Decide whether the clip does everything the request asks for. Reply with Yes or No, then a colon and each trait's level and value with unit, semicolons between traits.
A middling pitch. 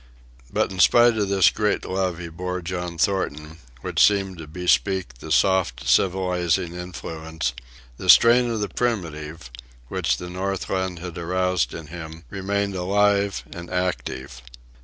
No: very low, 90 Hz